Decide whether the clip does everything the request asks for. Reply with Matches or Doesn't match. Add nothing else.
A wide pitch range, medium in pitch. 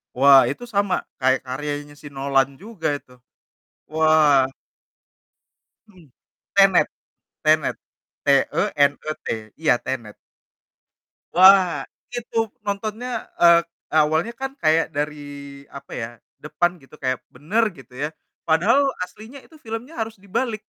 Matches